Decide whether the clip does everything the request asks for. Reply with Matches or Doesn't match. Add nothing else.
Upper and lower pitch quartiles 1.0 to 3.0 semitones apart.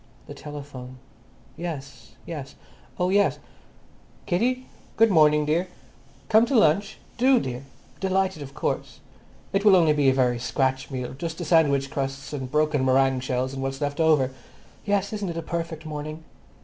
Doesn't match